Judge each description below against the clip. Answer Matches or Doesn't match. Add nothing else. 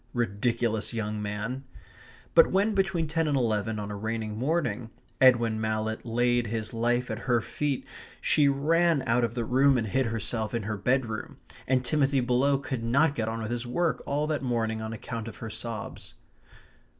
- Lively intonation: Doesn't match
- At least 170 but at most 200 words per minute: Matches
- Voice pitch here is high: Doesn't match